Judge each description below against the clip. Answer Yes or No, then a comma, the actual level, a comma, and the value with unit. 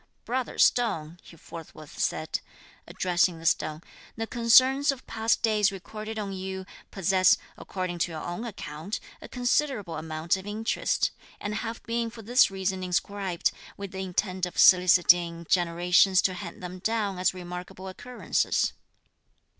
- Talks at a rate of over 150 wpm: No, average, 145 wpm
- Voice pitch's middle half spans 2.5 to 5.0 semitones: Yes, average, 3.9 semitones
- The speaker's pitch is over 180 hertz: Yes, high, 190 Hz